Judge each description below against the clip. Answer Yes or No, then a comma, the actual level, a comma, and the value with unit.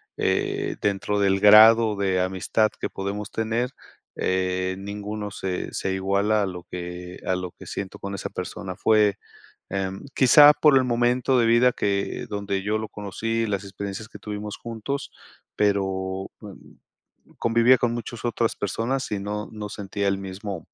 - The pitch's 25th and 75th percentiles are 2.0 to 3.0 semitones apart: Yes, average, 2.7 semitones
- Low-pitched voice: Yes, low, 105 Hz